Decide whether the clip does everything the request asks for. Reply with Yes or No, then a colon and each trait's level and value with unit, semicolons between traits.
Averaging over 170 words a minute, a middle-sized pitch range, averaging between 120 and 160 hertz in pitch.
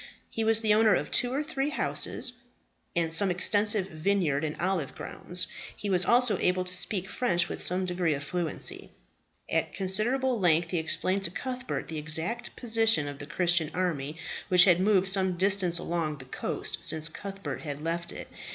No: average, 180 wpm; average, 4.1 semitones; medium, 185 Hz